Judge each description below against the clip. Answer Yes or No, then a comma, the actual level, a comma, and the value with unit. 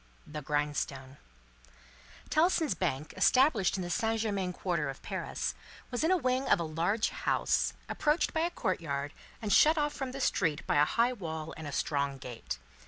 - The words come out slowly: No, average, 175 wpm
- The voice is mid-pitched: Yes, medium, 180 Hz